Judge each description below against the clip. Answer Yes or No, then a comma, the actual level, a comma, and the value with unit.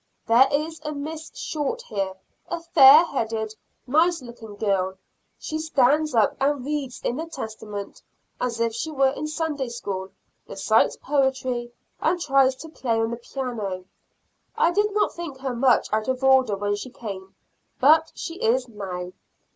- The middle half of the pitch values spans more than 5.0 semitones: Yes, wide, 5.4 semitones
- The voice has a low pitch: No, very high, 260 Hz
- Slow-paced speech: No, average, 160 wpm